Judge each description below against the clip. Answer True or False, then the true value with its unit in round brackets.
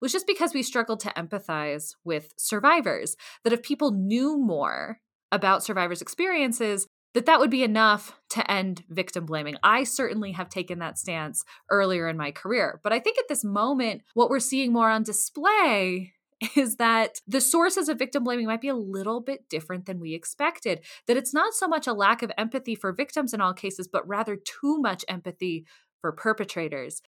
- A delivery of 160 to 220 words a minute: True (190 wpm)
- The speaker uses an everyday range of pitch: False (6.2 semitones)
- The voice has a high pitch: True (220 Hz)